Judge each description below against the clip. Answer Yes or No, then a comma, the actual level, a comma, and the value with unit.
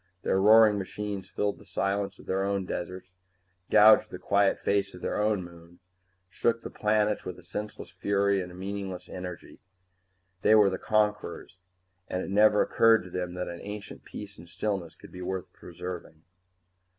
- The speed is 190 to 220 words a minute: No, average, 170 wpm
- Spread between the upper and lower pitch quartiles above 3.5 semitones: No, narrow, 2.4 semitones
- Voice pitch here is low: Yes, very low, 95 Hz